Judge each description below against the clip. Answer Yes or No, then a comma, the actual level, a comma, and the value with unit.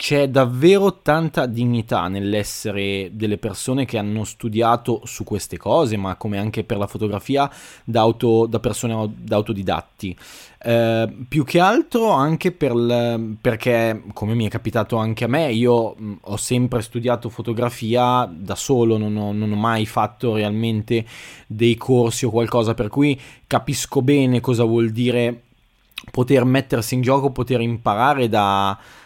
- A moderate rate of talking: Yes, average, 145 wpm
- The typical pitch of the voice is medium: No, low, 115 Hz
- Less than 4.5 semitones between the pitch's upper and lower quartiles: Yes, narrow, 2.6 semitones